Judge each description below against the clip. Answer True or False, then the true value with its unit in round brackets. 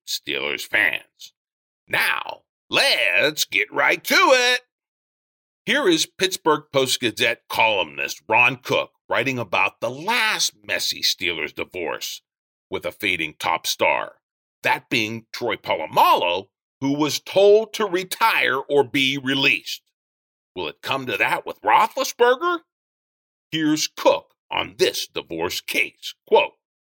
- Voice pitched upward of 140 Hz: True (190 Hz)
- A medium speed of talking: False (120 wpm)